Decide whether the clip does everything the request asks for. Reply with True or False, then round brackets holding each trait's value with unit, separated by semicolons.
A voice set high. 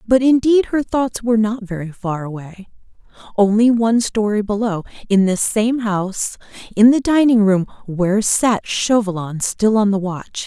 True (215 Hz)